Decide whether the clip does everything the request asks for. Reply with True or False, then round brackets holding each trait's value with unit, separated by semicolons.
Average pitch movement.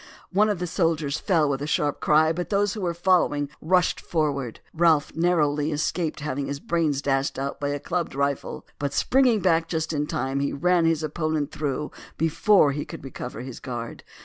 True (3.3 semitones)